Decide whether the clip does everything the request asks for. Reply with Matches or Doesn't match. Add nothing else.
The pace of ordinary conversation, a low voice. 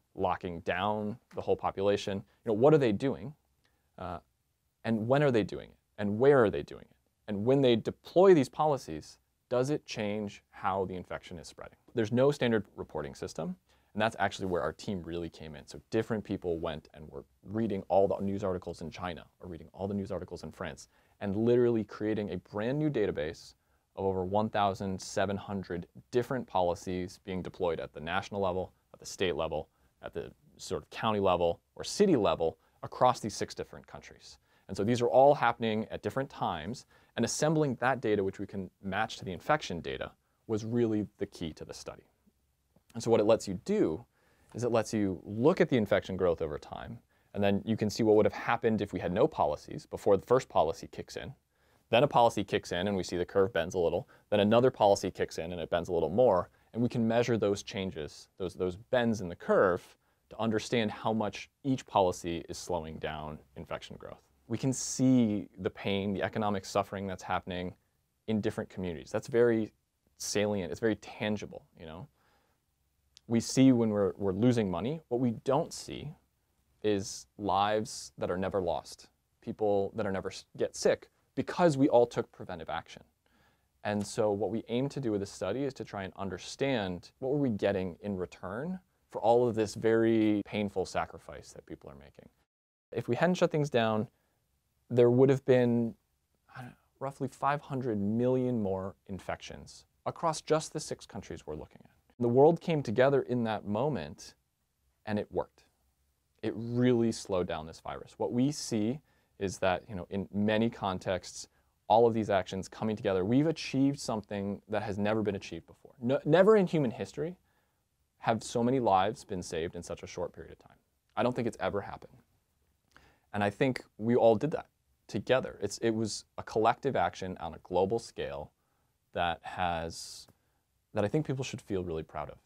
Matches